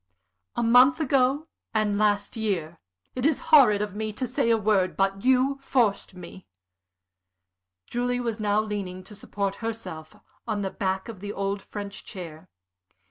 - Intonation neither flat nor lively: Yes, average, 3.9 semitones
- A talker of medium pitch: No, high, 210 Hz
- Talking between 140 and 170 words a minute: Yes, average, 155 wpm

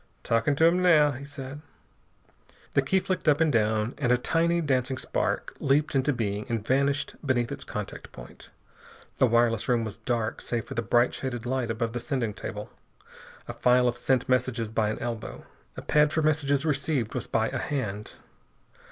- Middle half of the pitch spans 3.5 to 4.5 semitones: Yes, average, 3.9 semitones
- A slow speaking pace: No, average, 185 wpm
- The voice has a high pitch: No, low, 125 Hz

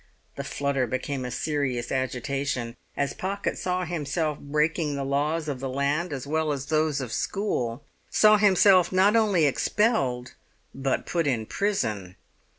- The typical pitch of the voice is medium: Yes, medium, 145 Hz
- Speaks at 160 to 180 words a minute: No, average, 150 wpm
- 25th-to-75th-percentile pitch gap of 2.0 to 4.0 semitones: No, average, 4.8 semitones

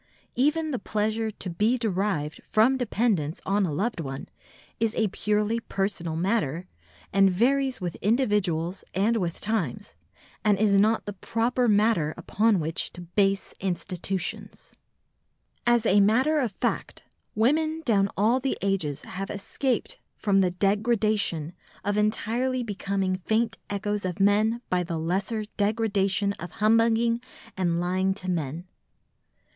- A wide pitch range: No, average, 3.6 semitones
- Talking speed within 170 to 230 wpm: No, slow, 135 wpm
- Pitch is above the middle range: Yes, high, 205 Hz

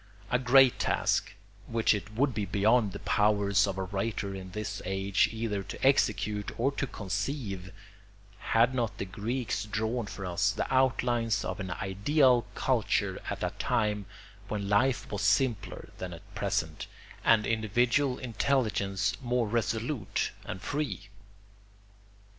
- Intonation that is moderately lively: Yes, average, 3.6 semitones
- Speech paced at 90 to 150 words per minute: Yes, average, 140 wpm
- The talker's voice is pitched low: Yes, low, 105 Hz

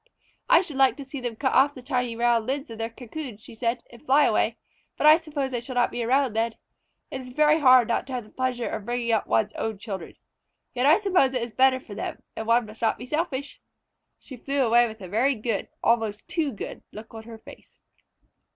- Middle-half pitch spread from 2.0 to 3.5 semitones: Yes, average, 3.1 semitones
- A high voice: Yes, high, 245 Hz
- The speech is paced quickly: Yes, fast, 235 wpm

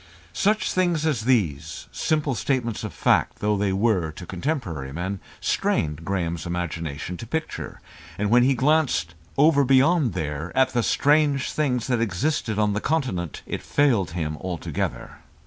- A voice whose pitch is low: Yes, low, 110 Hz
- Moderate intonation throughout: No, wide, 8.2 semitones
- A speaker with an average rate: Yes, average, 150 wpm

